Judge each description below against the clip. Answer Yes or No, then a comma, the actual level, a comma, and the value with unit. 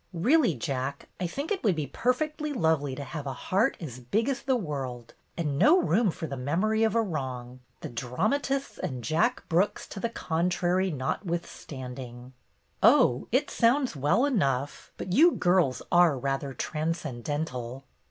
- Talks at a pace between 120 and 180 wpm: Yes, average, 160 wpm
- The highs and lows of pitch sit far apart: Yes, wide, 8.5 semitones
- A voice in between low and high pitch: Yes, medium, 160 Hz